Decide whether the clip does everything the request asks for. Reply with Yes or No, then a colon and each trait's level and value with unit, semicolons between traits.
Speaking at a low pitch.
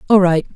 No: medium, 185 Hz